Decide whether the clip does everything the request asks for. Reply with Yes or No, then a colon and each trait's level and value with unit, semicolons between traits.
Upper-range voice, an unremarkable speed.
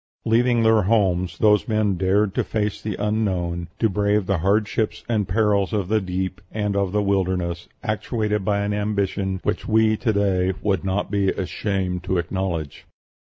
No: low, 100 Hz; average, 170 wpm